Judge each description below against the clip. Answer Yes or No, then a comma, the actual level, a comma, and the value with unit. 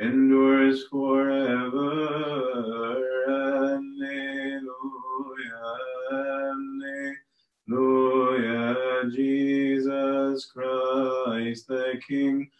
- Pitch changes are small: Yes, narrow, 1.1 semitones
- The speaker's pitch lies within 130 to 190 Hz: Yes, low, 135 Hz